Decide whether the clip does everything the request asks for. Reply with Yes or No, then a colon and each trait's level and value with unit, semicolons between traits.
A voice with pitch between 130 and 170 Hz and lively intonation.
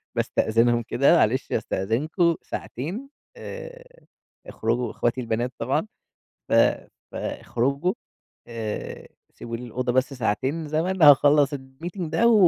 Yes: low, 135 Hz; wide, 5.9 semitones